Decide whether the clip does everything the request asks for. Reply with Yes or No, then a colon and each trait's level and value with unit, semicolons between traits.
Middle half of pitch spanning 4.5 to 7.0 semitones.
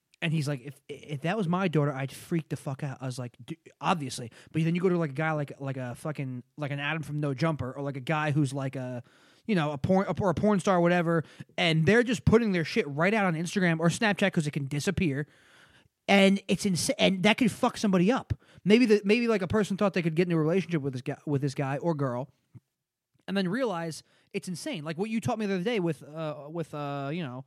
Yes: average, 5.1 semitones